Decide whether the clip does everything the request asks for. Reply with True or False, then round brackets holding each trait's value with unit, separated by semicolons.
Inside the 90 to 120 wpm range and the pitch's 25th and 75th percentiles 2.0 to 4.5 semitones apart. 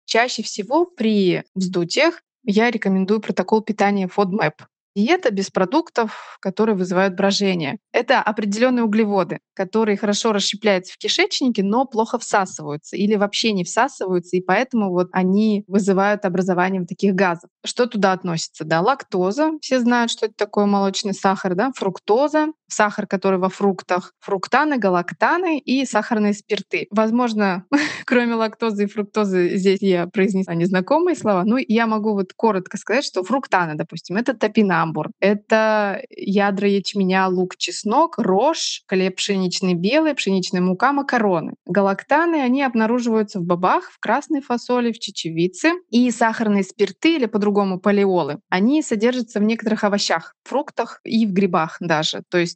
False (140 wpm; 3.6 semitones)